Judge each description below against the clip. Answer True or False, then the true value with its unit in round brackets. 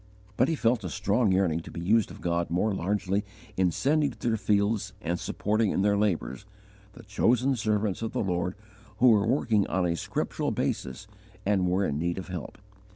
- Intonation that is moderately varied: True (3.5 semitones)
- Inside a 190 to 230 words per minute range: True (195 wpm)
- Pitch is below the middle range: True (100 Hz)